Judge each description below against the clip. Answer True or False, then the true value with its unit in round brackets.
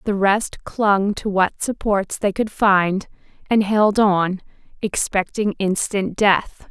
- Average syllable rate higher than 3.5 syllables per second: False (3.3 syllables/s)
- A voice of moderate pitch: False (200 Hz)